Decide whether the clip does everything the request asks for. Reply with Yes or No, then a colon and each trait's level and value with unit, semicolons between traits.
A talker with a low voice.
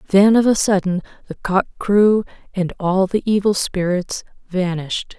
No: high, 190 Hz